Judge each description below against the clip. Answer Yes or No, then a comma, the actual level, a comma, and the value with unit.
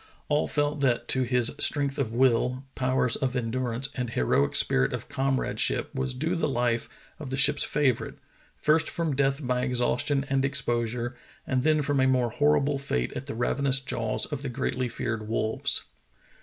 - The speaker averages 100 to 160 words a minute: No, average, 175 wpm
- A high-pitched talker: No, low, 130 Hz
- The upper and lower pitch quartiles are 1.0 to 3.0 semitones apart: Yes, narrow, 2.5 semitones